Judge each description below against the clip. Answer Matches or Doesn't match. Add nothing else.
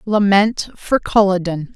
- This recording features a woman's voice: Matches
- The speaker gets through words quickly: Doesn't match